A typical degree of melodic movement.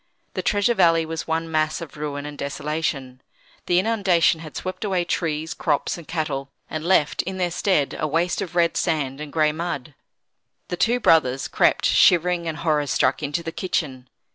Yes: average, 3.0 semitones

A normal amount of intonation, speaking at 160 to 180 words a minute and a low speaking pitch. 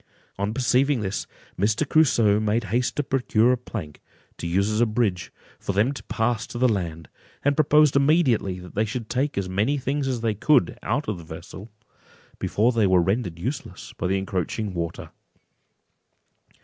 Yes: average, 4.8 semitones; average, 175 wpm; low, 110 Hz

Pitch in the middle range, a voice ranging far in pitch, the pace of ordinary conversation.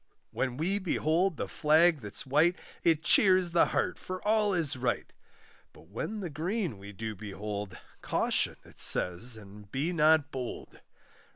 Yes: medium, 155 Hz; wide, 8.1 semitones; average, 155 wpm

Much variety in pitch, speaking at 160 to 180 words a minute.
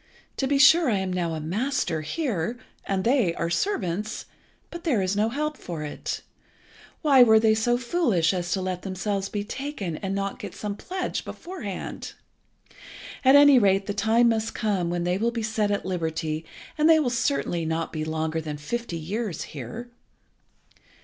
Yes: wide, 5.8 semitones; average, 175 wpm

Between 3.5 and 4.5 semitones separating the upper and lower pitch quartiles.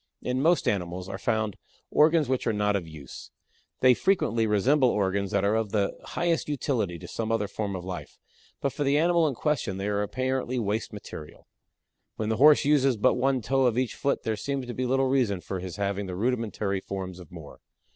No: average, 5.2 semitones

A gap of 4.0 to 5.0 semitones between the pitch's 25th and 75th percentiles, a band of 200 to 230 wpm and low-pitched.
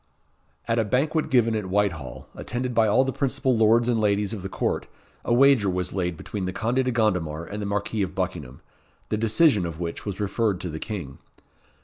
Yes: average, 4.5 semitones; fast, 205 wpm; low, 105 Hz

